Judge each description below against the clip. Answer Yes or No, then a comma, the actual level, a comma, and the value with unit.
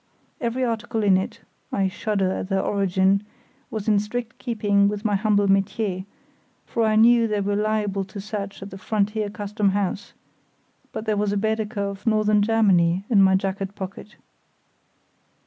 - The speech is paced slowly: No, average, 155 wpm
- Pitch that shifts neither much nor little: No, narrow, 1.7 semitones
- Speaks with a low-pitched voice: No, high, 205 Hz